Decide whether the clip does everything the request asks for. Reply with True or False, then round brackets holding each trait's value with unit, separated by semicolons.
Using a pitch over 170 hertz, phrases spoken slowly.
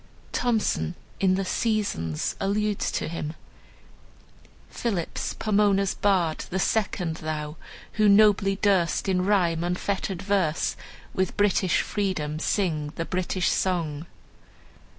True (190 Hz; 110 wpm)